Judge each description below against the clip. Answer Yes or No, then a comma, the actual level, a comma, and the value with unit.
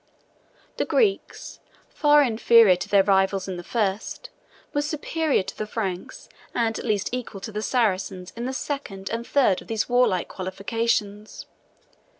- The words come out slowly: No, average, 155 wpm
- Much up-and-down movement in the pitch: No, average, 4.4 semitones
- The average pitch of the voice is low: No, high, 220 Hz